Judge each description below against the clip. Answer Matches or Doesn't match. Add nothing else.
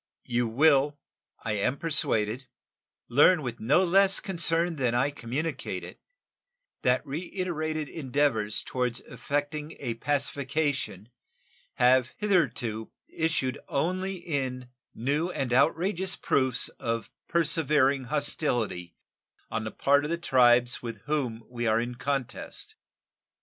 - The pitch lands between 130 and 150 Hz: Matches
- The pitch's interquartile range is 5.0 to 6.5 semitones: Doesn't match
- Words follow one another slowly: Matches